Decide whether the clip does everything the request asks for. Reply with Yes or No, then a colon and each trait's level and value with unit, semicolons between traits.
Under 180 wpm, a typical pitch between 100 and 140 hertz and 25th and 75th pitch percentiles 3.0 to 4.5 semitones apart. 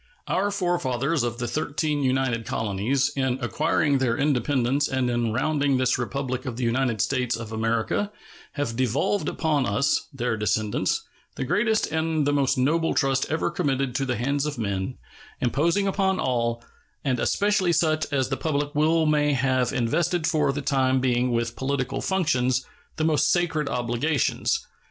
Yes: average, 160 wpm; low, 135 Hz; average, 3.9 semitones